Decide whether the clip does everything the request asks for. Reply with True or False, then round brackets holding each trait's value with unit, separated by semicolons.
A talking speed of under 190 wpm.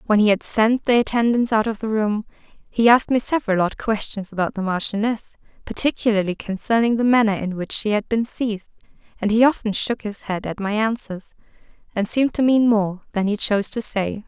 False (200 wpm)